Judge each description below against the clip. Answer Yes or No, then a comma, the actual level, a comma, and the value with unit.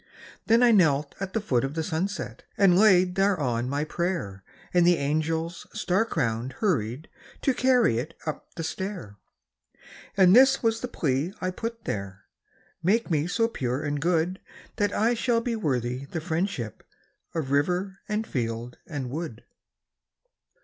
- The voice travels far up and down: Yes, wide, 6.7 semitones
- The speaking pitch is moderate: Yes, medium, 170 Hz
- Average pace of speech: Yes, average, 155 wpm